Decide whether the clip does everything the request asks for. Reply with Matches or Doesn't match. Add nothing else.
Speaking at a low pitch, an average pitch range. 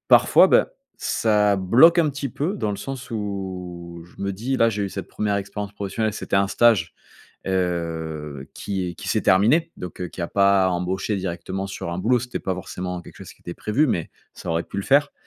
Matches